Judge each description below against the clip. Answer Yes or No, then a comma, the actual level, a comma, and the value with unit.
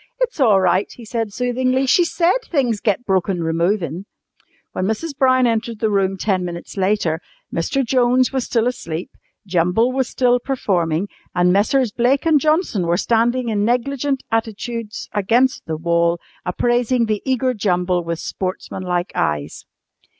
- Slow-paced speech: No, average, 150 wpm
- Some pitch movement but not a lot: No, wide, 5.8 semitones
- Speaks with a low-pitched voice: No, high, 220 Hz